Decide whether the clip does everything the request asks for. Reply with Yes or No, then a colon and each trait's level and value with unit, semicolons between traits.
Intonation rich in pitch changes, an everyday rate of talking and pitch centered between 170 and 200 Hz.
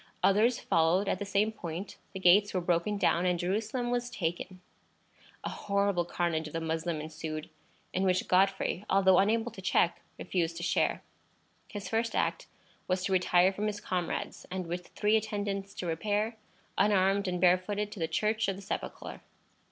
No: average, 2.9 semitones; average, 170 wpm; high, 190 Hz